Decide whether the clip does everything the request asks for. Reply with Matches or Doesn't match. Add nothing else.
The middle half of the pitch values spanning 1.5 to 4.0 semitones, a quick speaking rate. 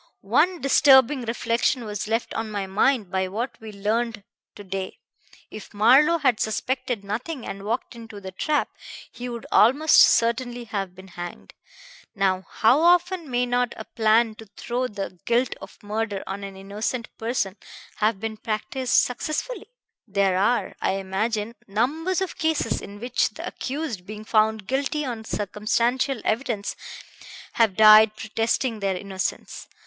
Doesn't match